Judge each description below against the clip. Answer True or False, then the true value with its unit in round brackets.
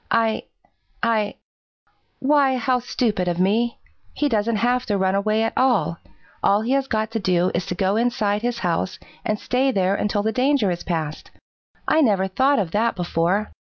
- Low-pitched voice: False (215 Hz)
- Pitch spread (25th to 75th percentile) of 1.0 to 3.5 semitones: False (4.4 semitones)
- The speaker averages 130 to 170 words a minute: False (180 wpm)